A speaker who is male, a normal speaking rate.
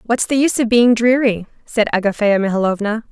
No: female; average, 175 wpm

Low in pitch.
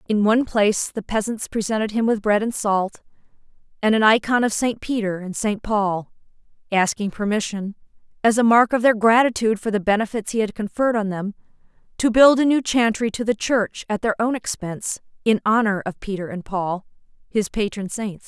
No: high, 215 Hz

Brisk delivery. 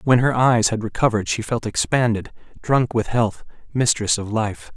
No: average, 175 wpm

